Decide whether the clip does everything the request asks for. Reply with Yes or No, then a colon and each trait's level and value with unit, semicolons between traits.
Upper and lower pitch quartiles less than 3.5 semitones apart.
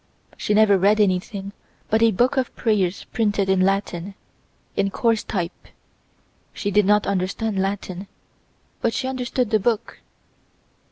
Yes: narrow, 2.5 semitones